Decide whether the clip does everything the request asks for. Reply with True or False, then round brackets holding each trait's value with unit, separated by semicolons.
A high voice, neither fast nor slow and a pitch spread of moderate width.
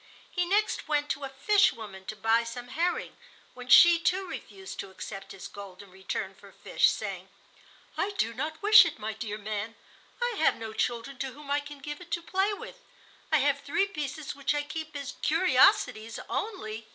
False (285 Hz; 195 wpm; 7.3 semitones)